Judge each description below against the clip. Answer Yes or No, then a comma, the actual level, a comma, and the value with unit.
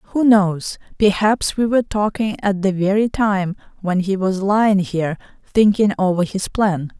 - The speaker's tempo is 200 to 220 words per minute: No, average, 165 wpm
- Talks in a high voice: Yes, high, 200 Hz